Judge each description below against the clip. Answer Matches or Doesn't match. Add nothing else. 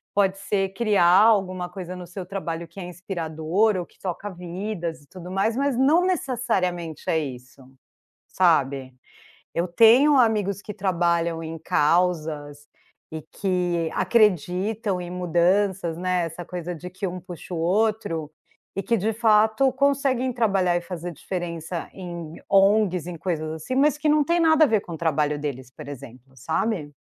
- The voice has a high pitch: Doesn't match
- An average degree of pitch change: Matches